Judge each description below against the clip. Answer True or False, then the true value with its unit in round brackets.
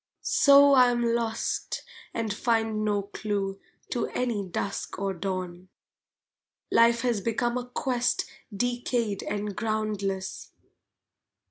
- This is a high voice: True (220 Hz)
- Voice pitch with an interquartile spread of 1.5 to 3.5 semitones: True (3.2 semitones)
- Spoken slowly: True (110 wpm)